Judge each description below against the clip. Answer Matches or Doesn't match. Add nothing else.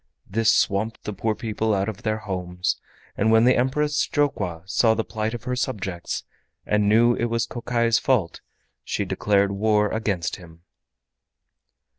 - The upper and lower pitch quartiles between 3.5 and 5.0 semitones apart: Doesn't match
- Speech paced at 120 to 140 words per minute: Doesn't match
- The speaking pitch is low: Matches